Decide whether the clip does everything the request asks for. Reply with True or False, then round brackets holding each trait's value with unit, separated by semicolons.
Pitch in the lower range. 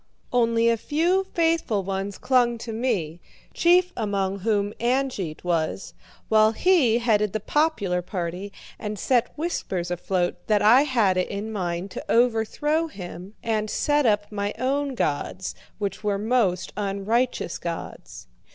False (215 Hz)